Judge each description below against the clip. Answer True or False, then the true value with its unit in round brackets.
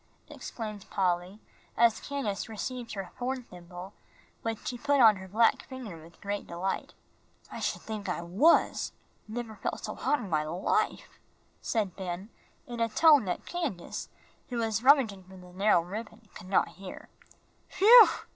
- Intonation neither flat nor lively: True (4.7 semitones)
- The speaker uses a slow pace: False (160 wpm)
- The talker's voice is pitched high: True (215 Hz)